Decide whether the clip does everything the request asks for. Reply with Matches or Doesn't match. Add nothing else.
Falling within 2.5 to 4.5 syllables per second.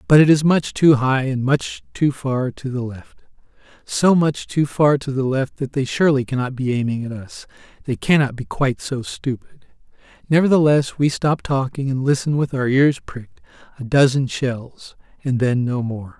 Doesn't match